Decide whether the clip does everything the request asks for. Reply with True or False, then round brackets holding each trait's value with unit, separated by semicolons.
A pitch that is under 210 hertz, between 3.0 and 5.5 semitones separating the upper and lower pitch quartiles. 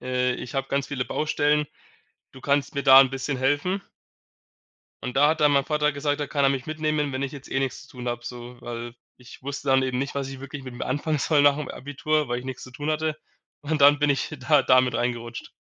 False (140 Hz; 2.4 semitones)